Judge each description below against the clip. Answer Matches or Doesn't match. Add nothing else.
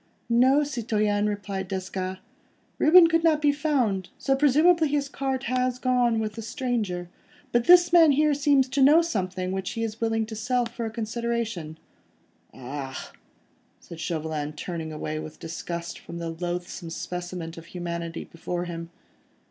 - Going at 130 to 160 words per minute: Matches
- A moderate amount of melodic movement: Doesn't match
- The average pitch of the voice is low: Doesn't match